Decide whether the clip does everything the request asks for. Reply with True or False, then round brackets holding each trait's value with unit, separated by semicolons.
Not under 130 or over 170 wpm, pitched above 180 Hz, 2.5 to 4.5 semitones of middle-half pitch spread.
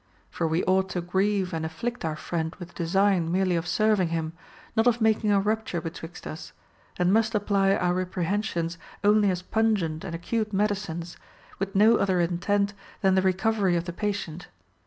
False (180 wpm; 190 Hz; 3.3 semitones)